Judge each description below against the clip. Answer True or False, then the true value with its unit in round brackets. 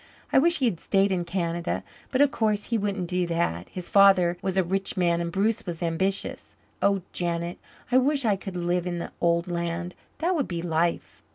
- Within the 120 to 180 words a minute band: False (205 wpm)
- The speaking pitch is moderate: True (180 Hz)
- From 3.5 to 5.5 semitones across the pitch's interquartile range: False (2.7 semitones)